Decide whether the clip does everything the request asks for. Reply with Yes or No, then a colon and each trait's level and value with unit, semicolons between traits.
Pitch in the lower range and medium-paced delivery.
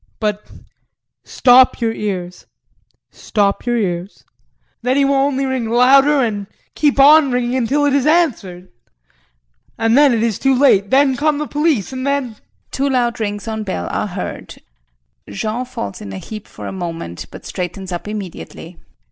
No: high, 240 Hz; average, 160 wpm